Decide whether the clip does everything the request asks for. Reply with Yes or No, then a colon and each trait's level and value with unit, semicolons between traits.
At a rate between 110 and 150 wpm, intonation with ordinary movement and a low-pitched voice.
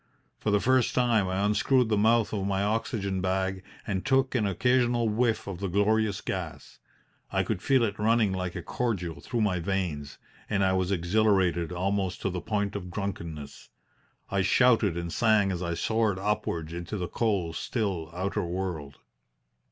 No: average, 170 wpm; average, 3.3 semitones; low, 100 Hz